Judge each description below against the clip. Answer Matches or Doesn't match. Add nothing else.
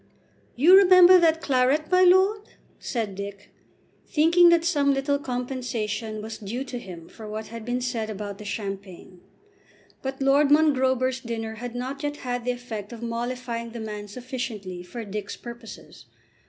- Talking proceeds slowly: Doesn't match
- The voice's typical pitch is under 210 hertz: Doesn't match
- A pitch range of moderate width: Matches